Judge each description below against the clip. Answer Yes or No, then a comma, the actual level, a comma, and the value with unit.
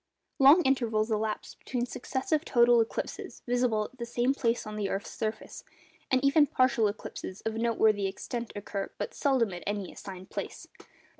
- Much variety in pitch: No, average, 3.3 semitones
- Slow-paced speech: No, average, 160 wpm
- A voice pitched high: Yes, high, 230 Hz